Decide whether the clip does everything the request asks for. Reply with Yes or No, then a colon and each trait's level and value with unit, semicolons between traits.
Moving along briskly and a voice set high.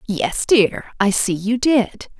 No: average, 165 wpm; high, 215 Hz